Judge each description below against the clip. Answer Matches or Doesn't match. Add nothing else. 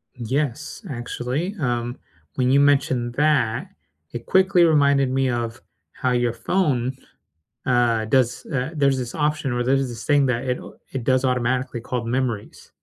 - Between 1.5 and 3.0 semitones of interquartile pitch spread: Matches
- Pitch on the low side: Matches